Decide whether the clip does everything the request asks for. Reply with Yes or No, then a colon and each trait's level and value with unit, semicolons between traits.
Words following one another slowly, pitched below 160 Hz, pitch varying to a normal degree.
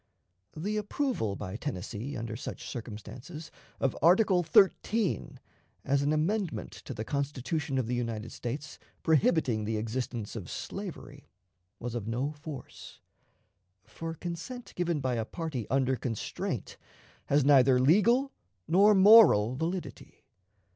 No: slow, 125 wpm; medium, 140 Hz; wide, 6.5 semitones